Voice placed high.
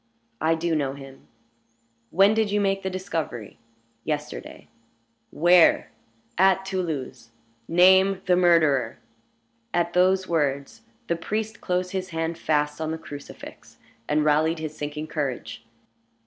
No: medium, 165 Hz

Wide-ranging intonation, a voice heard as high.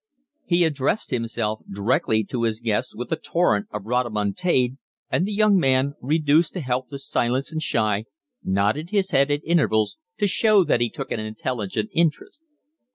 No: wide, 6.9 semitones; low, 130 Hz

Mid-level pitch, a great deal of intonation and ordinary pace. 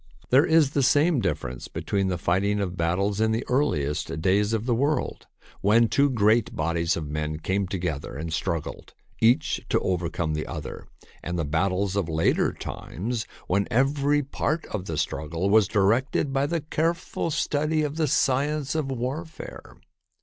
No: low, 105 Hz; wide, 8.5 semitones; average, 170 wpm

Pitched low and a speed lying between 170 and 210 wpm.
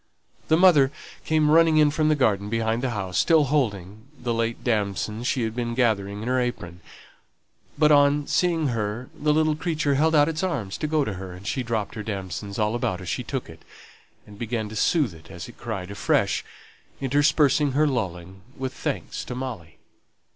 Yes: low, 120 Hz; average, 190 wpm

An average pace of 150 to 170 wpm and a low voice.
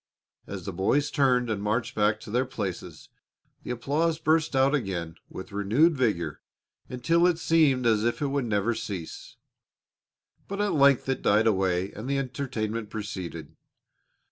Yes: average, 155 wpm; low, 120 Hz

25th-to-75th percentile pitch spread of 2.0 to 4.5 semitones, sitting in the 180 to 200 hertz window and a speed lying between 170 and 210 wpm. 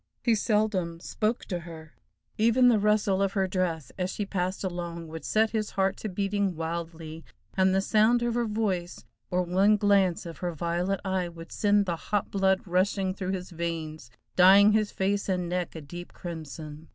Yes: average, 3.0 semitones; medium, 185 Hz; average, 185 wpm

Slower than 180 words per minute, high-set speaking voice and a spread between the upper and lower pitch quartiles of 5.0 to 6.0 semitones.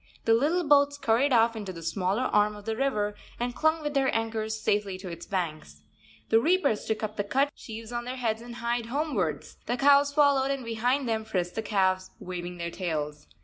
No: fast, 205 wpm; high, 225 Hz; wide, 5.4 semitones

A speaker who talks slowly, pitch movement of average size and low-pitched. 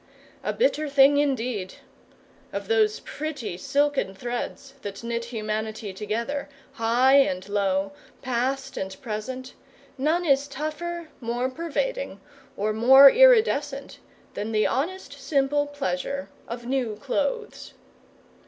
No: slow, 115 wpm; average, 4.8 semitones; very high, 260 Hz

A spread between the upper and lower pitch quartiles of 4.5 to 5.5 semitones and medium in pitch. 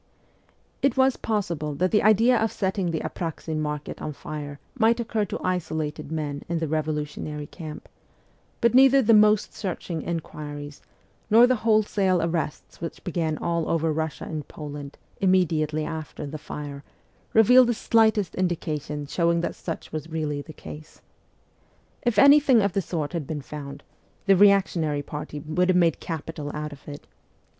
Yes: average, 5.0 semitones; medium, 165 Hz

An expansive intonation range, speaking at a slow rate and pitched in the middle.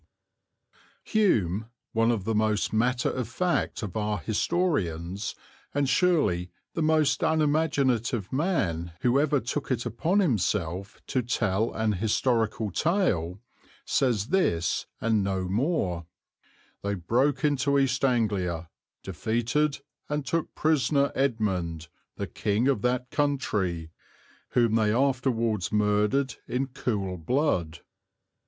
No: wide, 5.9 semitones; slow, 120 wpm; low, 115 Hz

